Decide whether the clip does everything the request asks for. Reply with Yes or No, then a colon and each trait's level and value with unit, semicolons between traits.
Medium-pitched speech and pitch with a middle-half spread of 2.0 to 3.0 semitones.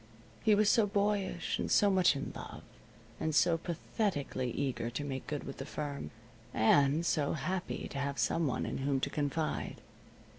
No: medium, 150 Hz; average, 4.8 semitones